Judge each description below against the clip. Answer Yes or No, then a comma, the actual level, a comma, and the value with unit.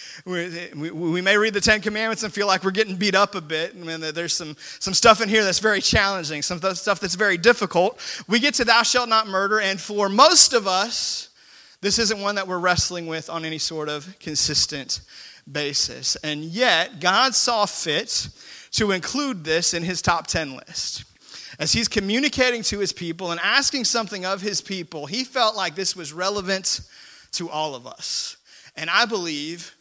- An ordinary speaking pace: Yes, average, 190 wpm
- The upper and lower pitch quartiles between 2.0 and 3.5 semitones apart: No, average, 4.3 semitones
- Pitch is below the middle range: No, high, 195 Hz